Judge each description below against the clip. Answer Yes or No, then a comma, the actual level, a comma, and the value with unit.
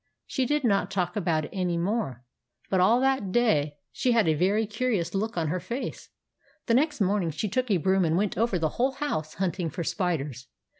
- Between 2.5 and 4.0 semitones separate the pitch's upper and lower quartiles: No, wide, 5.4 semitones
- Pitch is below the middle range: No, high, 190 Hz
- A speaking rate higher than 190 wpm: Yes, fast, 205 wpm